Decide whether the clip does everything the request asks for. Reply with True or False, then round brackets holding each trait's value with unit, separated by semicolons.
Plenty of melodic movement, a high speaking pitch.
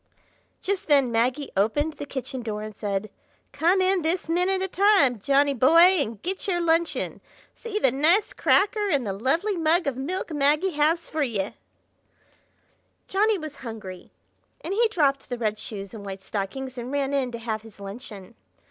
True (7.3 semitones; 280 Hz)